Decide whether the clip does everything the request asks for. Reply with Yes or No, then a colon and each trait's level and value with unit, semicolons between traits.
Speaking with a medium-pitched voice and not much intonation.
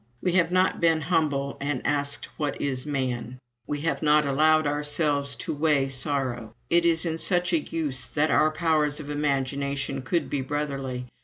Yes: medium, 145 Hz; narrow, 2.3 semitones